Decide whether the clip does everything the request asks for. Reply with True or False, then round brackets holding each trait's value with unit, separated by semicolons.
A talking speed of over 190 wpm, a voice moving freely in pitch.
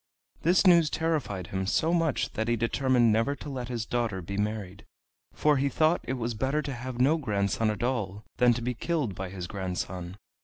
True (200 wpm; 5.7 semitones)